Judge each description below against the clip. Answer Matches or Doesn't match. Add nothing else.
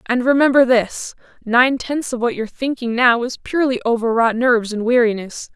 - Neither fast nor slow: Matches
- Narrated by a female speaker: Matches